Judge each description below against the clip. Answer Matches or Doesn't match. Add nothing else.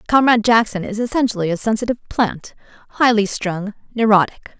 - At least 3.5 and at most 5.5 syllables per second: Doesn't match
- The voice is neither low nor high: Doesn't match